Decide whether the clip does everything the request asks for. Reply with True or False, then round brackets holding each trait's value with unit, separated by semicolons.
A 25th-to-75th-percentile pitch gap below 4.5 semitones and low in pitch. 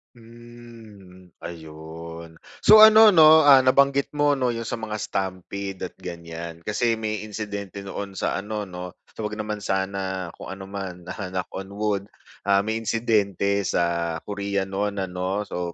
True (3.3 semitones; 100 Hz)